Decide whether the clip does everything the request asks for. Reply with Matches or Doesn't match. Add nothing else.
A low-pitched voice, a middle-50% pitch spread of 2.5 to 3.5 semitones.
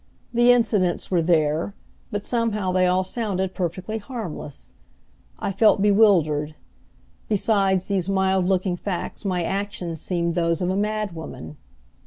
Doesn't match